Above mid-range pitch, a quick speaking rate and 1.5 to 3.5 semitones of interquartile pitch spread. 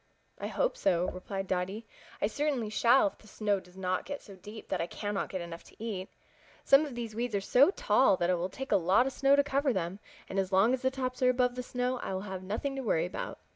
No: high, 215 Hz; fast, 255 wpm; wide, 5.4 semitones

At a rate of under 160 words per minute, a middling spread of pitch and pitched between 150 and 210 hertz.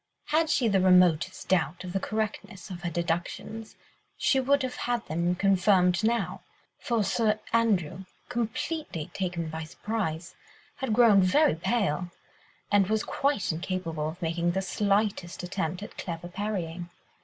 Yes: average, 145 wpm; average, 4.1 semitones; high, 190 Hz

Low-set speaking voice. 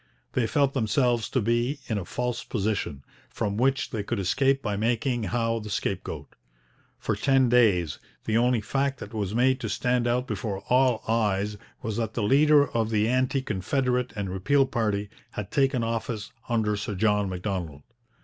Yes: low, 115 Hz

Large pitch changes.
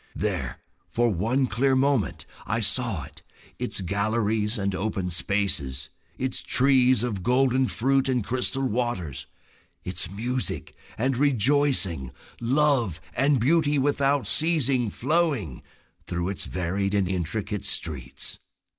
Yes: wide, 5.8 semitones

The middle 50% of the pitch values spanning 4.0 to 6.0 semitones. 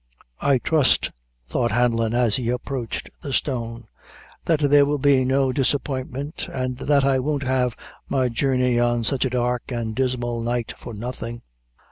No: narrow, 2.4 semitones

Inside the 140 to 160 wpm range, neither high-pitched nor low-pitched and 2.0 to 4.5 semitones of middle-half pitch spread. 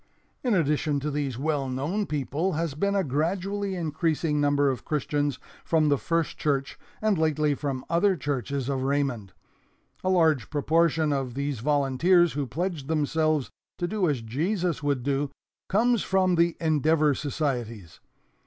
Yes: average, 150 wpm; medium, 150 Hz; average, 3.4 semitones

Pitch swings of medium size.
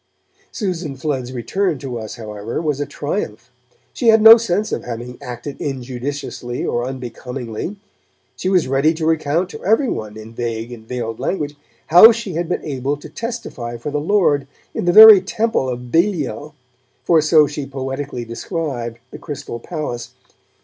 No: wide, 6.0 semitones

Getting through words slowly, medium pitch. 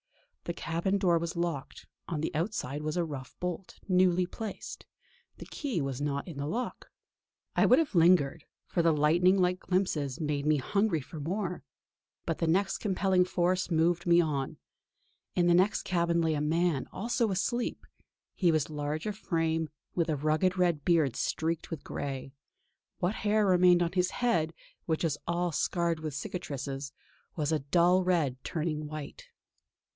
No: average, 165 wpm; medium, 170 Hz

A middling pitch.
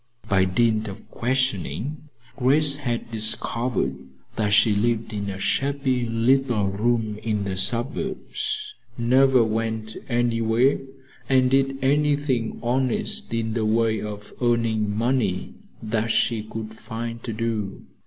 No: low, 115 Hz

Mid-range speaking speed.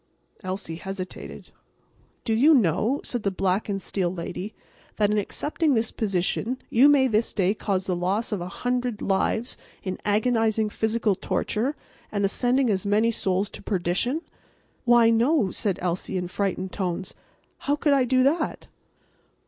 Yes: average, 155 wpm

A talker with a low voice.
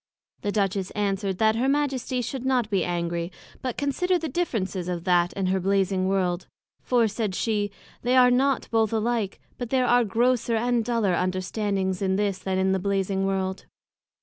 No: high, 205 Hz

